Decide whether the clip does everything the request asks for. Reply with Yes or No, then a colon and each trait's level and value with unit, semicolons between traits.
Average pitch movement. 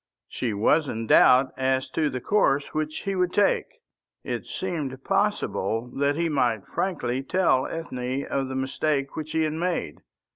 Yes: average, 3.8 semitones